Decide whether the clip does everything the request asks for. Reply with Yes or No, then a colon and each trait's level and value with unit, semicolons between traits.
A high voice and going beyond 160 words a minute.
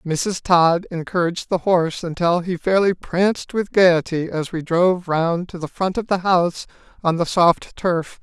No: medium, 175 Hz; average, 180 wpm